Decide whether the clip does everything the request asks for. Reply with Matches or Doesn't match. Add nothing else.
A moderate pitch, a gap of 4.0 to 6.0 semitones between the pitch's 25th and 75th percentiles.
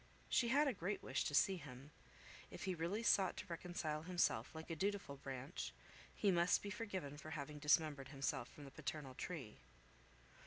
Matches